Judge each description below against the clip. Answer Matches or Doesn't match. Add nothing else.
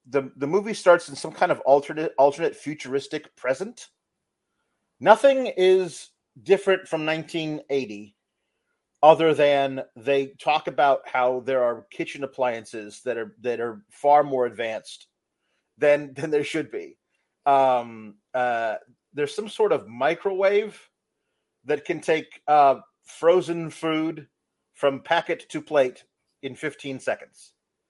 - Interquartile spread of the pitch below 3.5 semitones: Doesn't match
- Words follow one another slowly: Matches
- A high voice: Doesn't match